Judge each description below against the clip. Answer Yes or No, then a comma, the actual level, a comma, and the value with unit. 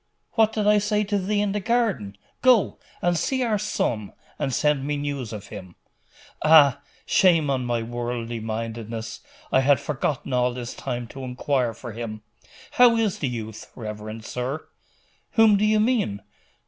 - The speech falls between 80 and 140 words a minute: No, average, 165 wpm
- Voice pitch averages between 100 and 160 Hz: Yes, low, 135 Hz